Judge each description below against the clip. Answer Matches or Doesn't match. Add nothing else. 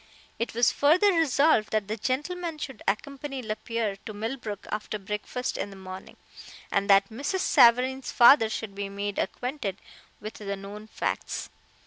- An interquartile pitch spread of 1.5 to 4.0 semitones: Doesn't match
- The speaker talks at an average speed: Matches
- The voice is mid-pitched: Doesn't match